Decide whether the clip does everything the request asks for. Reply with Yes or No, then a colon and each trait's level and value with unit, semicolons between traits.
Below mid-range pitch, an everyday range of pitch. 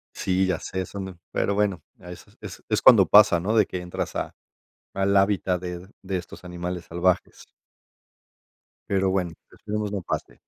No: very low, 95 Hz; narrow, 1.9 semitones